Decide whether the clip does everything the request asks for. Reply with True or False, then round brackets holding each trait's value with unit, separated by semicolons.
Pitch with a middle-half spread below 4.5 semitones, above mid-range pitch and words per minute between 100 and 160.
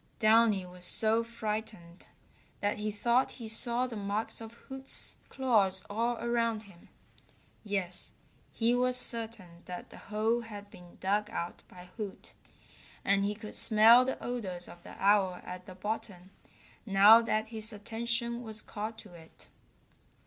True (2.9 semitones; 215 Hz; 150 wpm)